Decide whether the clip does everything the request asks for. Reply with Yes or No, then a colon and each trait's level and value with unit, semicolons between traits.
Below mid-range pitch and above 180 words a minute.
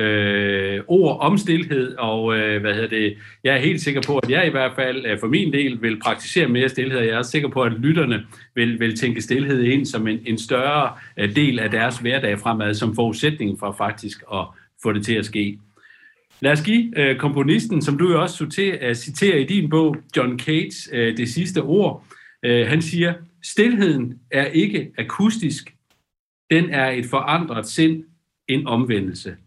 No: low, 130 Hz; average, 175 wpm